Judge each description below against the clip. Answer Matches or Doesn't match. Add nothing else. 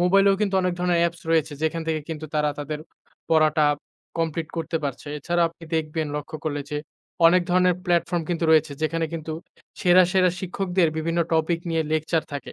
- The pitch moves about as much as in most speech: Doesn't match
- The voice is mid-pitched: Matches